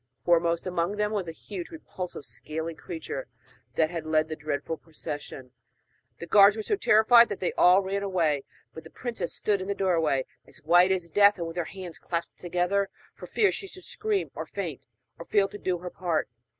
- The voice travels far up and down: No, average, 3.7 semitones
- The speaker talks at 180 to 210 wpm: Yes, average, 200 wpm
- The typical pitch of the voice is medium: Yes, medium, 180 Hz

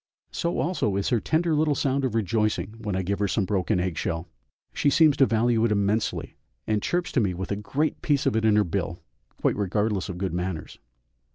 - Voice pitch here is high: No, low, 105 Hz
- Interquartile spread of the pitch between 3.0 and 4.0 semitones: No, wide, 5.5 semitones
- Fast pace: Yes, fast, 215 wpm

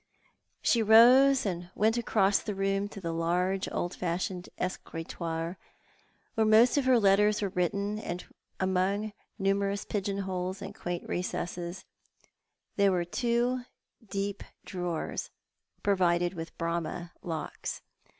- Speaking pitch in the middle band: No, high, 195 Hz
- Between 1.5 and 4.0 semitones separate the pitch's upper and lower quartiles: Yes, average, 2.9 semitones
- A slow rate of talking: Yes, slow, 125 wpm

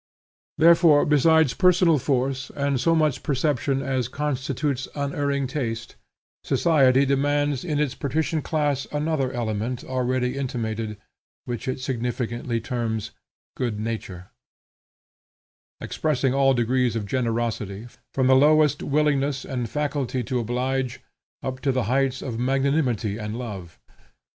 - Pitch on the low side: Yes, low, 130 Hz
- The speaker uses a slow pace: Yes, slow, 120 wpm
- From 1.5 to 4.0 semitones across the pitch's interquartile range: Yes, average, 3.2 semitones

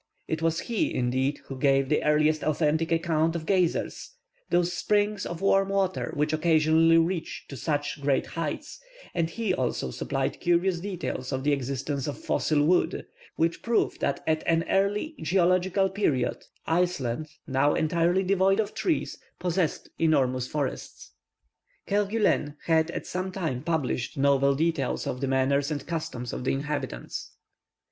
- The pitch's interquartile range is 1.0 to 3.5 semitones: No, average, 4.4 semitones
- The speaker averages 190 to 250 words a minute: No, average, 150 wpm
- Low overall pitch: No, medium, 160 Hz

